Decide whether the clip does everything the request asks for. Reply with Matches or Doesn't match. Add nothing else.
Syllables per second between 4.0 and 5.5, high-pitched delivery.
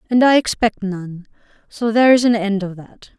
Matches